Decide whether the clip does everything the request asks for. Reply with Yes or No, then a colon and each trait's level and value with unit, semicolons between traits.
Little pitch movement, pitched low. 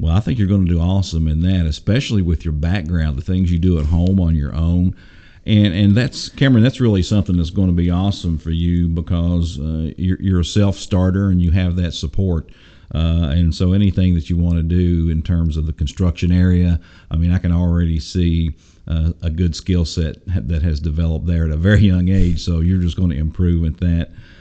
Yes: narrow, 2.1 semitones; very low, 85 Hz